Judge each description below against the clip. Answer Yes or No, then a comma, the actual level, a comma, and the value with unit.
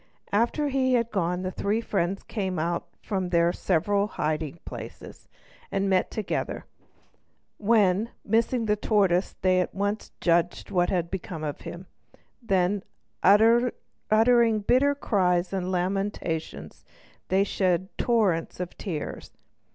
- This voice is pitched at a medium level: No, high, 195 Hz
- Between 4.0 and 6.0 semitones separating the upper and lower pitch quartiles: No, average, 3.4 semitones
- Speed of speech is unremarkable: No, slow, 125 wpm